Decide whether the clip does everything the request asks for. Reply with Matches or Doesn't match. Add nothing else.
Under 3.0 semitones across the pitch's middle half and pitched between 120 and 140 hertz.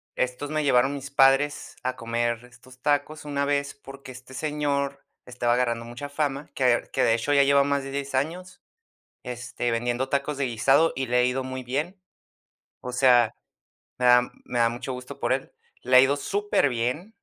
Matches